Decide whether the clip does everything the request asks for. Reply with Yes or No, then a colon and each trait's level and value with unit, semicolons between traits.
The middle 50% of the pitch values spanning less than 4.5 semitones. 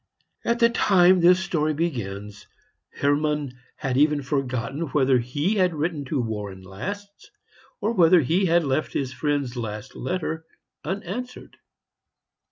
No: wide, 5.6 semitones